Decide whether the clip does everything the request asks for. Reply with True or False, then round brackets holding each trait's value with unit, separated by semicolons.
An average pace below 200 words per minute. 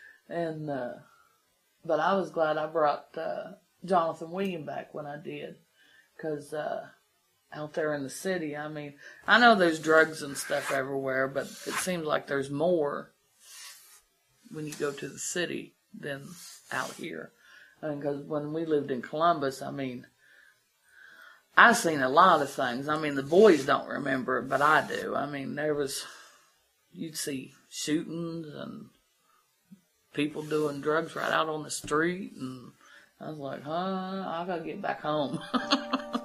True (165 wpm)